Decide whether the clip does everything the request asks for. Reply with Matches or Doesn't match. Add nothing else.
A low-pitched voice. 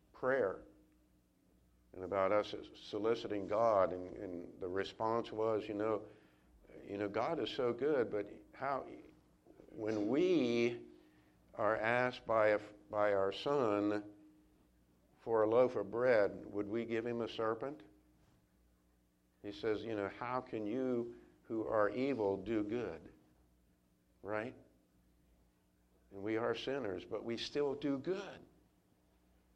Matches